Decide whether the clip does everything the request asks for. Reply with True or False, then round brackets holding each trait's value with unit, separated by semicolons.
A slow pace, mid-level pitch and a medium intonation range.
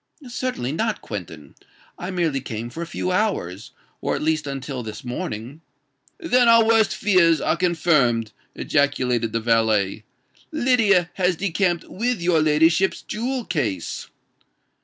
False (130 wpm; 160 Hz; 8.6 semitones)